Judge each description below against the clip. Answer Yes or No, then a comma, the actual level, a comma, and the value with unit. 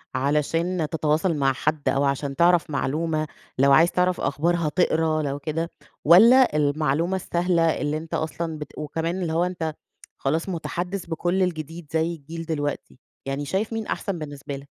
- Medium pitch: Yes, medium, 160 Hz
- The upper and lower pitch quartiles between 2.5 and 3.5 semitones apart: Yes, average, 2.9 semitones